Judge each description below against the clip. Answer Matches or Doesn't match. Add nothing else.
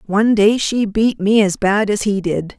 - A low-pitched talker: Doesn't match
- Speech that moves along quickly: Matches